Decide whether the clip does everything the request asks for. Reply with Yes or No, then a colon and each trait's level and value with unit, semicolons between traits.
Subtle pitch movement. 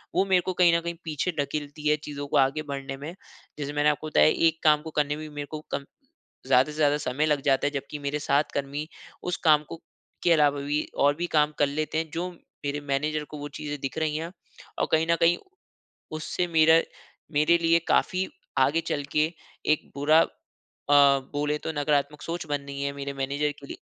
Yes: narrow, 1.9 semitones